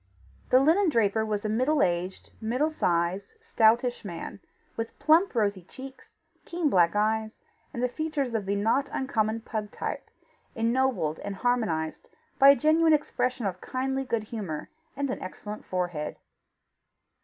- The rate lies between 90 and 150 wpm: Yes, average, 145 wpm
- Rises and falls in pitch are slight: No, average, 5.0 semitones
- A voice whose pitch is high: Yes, high, 225 Hz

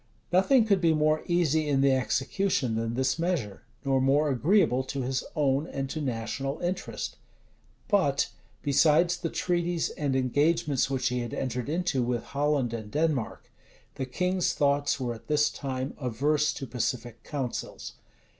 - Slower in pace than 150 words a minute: No, average, 155 wpm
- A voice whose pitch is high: No, medium, 140 Hz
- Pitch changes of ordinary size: Yes, average, 3.8 semitones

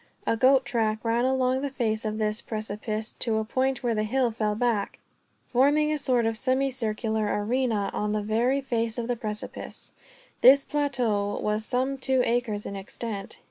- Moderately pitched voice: No, high, 230 Hz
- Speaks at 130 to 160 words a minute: No, average, 175 wpm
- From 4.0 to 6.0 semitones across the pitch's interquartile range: No, average, 3.2 semitones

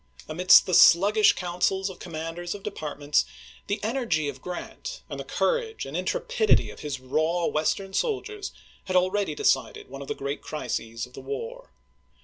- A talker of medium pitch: Yes, medium, 180 Hz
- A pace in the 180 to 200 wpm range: No, average, 165 wpm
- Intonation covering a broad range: Yes, wide, 6.8 semitones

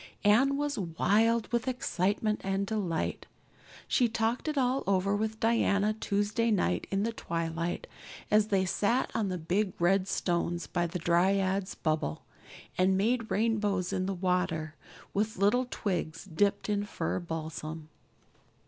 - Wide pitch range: No, average, 3.8 semitones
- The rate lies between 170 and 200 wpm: No, average, 140 wpm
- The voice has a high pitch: Yes, high, 200 Hz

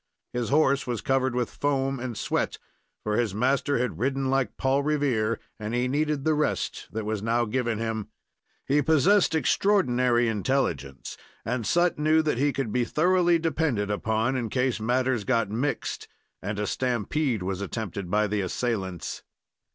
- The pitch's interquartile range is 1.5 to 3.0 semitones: No, average, 4.3 semitones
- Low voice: Yes, low, 125 Hz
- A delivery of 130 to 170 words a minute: Yes, average, 160 wpm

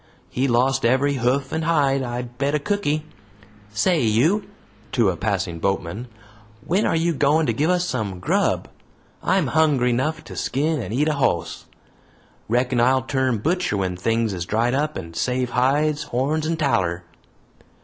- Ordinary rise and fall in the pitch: Yes, average, 4.8 semitones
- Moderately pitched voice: No, low, 130 Hz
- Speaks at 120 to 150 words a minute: No, average, 165 wpm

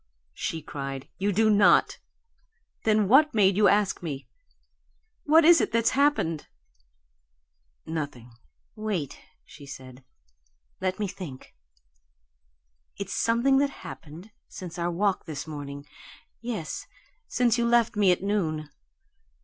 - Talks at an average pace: No, slow, 125 wpm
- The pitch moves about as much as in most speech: No, wide, 6.4 semitones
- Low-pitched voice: No, high, 190 Hz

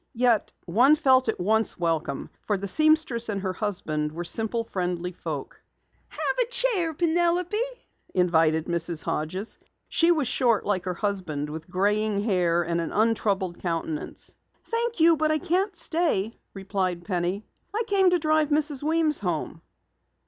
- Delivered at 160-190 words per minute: No, average, 150 wpm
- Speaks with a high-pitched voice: Yes, high, 210 Hz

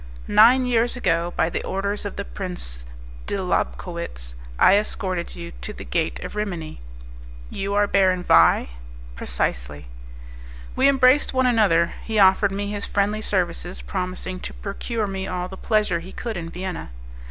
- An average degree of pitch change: Yes, average, 3.7 semitones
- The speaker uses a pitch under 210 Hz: Yes, high, 190 Hz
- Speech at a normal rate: Yes, average, 155 wpm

